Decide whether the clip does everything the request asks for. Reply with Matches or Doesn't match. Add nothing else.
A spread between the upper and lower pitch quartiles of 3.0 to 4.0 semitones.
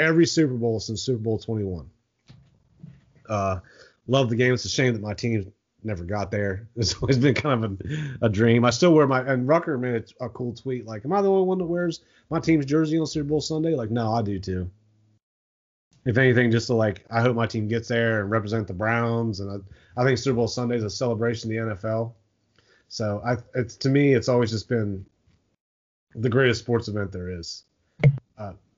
Matches